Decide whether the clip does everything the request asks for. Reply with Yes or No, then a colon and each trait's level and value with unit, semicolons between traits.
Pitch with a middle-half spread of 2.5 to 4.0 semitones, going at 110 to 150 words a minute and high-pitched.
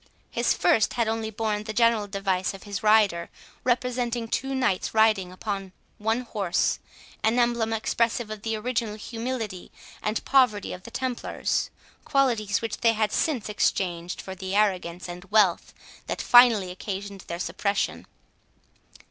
Yes: average, 3.0 semitones; average, 145 wpm; high, 215 Hz